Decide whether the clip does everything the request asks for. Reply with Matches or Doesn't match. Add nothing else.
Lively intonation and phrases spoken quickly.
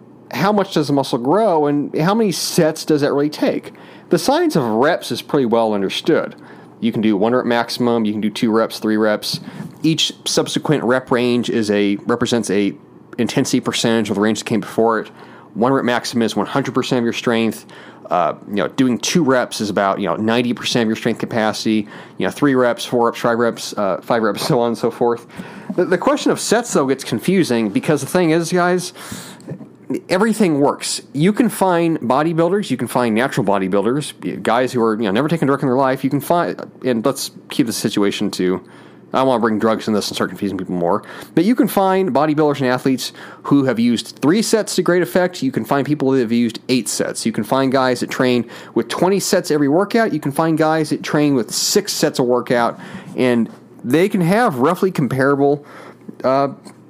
Matches